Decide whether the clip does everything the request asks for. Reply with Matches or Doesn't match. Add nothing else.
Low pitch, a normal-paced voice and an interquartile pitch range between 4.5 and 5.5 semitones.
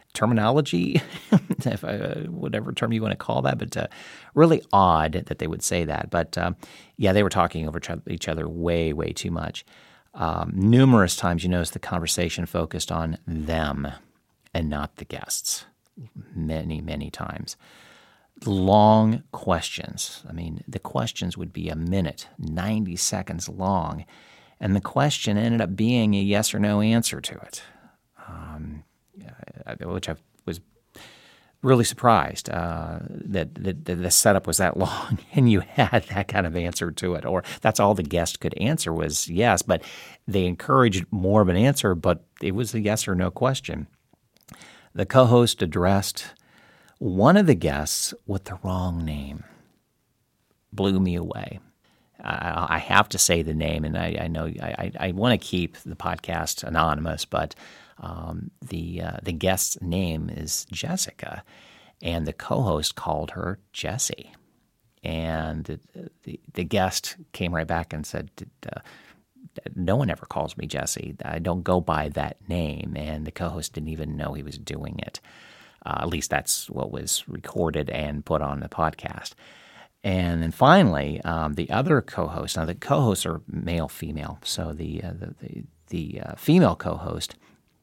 Doesn't match